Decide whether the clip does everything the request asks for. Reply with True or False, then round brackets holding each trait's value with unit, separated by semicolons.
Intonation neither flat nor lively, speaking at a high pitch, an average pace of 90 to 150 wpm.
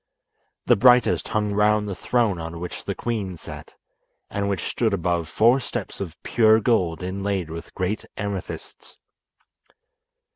False (3.4 semitones; 100 Hz; 140 wpm)